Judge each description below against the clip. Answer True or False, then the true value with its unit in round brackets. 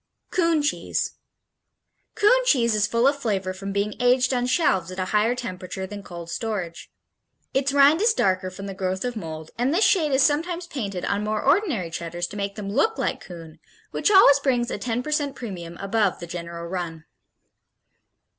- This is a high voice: True (210 Hz)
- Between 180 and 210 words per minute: True (185 wpm)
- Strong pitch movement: True (7.0 semitones)